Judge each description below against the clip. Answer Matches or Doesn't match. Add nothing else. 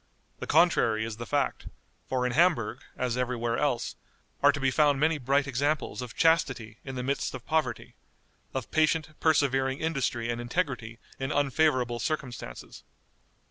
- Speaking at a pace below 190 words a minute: Matches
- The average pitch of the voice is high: Doesn't match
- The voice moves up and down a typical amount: Matches